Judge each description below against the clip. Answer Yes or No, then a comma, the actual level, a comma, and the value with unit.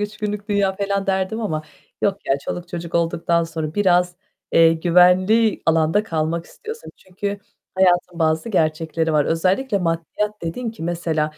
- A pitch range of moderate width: Yes, average, 3.6 semitones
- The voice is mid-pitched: Yes, medium, 180 Hz